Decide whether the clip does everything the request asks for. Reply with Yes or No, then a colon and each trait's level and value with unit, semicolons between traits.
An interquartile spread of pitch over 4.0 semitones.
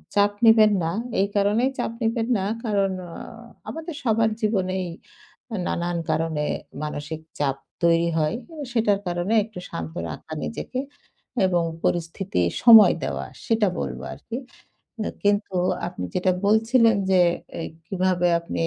Yes: average, 4.7 semitones